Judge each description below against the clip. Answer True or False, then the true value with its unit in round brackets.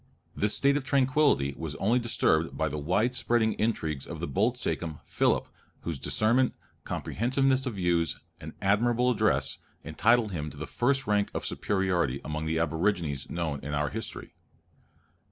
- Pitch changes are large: True (7.4 semitones)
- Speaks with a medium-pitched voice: False (100 Hz)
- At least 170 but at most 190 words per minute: False (155 wpm)